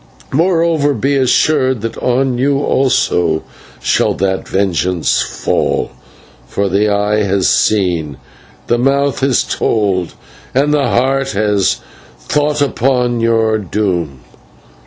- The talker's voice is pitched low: Yes, low, 115 Hz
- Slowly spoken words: Yes, slow, 115 wpm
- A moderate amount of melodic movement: No, wide, 5.7 semitones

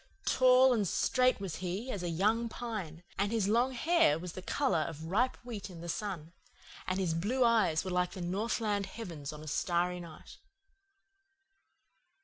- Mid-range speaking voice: No, high, 195 Hz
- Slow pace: No, average, 170 wpm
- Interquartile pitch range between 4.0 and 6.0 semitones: Yes, average, 5.2 semitones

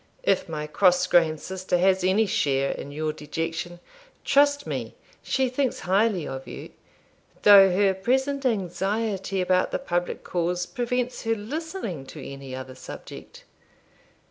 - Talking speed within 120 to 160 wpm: Yes, average, 140 wpm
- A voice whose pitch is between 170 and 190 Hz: Yes, medium, 185 Hz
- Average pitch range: No, wide, 5.7 semitones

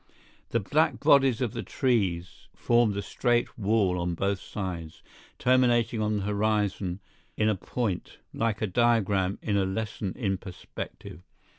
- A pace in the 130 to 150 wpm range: Yes, average, 145 wpm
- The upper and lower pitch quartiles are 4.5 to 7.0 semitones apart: No, average, 3.7 semitones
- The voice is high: No, low, 105 Hz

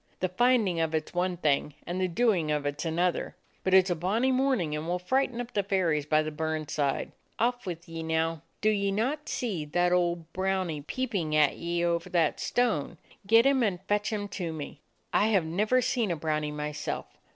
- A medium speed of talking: No, fast, 215 wpm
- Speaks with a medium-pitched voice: Yes, medium, 175 Hz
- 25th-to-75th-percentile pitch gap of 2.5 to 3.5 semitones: No, average, 4.8 semitones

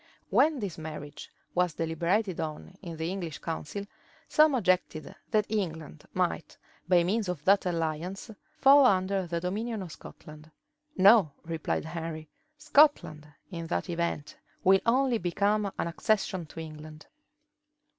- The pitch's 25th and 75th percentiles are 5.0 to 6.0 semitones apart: No, average, 4.2 semitones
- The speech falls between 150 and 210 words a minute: No, slow, 135 wpm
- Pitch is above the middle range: No, medium, 180 Hz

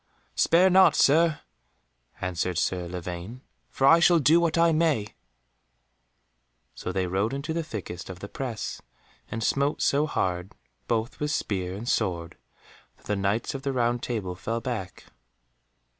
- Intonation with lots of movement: Yes, wide, 8.0 semitones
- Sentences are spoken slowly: No, average, 150 wpm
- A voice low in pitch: Yes, low, 115 Hz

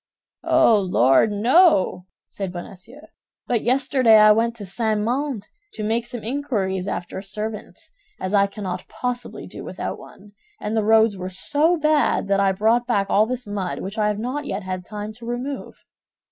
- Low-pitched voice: No, high, 215 Hz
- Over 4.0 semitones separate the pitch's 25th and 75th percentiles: No, average, 3.6 semitones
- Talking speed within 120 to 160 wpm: No, average, 175 wpm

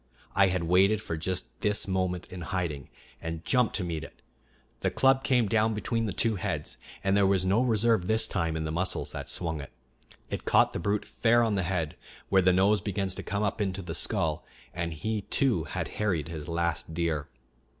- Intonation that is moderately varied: Yes, average, 4.0 semitones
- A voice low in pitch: Yes, very low, 95 Hz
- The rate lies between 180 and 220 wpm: Yes, fast, 205 wpm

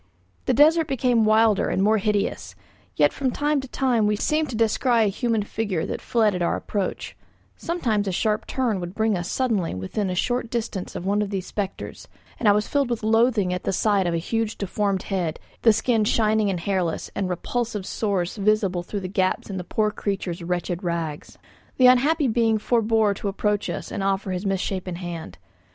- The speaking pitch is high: Yes, high, 210 Hz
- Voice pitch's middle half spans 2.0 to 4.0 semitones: Yes, average, 3.4 semitones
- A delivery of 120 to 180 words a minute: No, average, 200 wpm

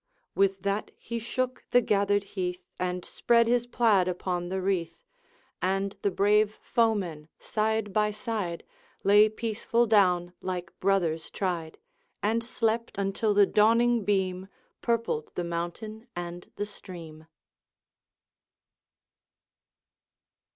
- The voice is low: No, high, 200 Hz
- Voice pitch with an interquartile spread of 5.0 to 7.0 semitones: No, average, 3.5 semitones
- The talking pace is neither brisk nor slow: No, slow, 115 wpm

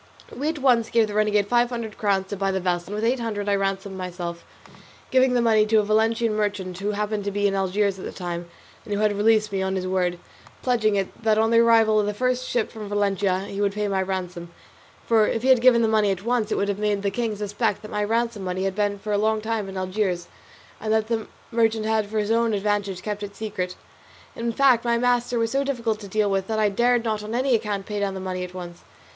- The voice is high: Yes, high, 210 Hz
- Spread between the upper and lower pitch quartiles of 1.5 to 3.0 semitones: Yes, narrow, 2.5 semitones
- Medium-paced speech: No, fast, 255 wpm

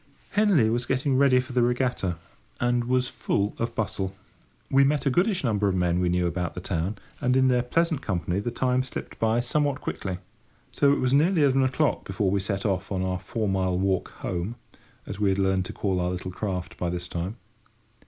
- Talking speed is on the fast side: Yes, fast, 210 wpm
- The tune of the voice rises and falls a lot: Yes, wide, 5.7 semitones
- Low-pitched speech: Yes, low, 110 Hz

